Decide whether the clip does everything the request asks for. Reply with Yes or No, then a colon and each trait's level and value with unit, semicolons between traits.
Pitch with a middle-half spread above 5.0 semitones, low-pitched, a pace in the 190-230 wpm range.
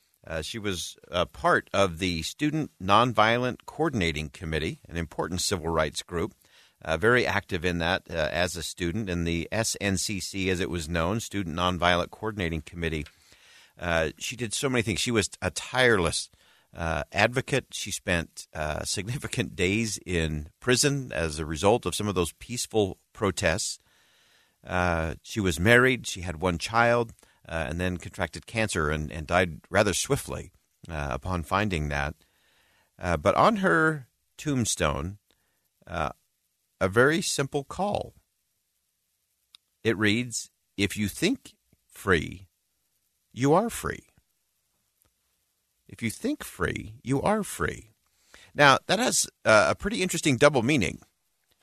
No: wide, 5.6 semitones; very low, 95 Hz; average, 140 wpm